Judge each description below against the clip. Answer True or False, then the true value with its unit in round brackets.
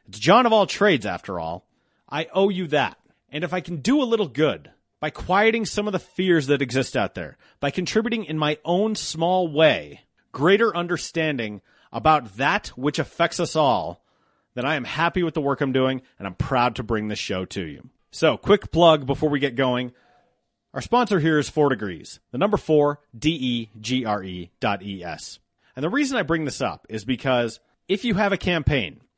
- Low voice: False (150 Hz)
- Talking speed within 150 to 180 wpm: False (205 wpm)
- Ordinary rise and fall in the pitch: False (6.0 semitones)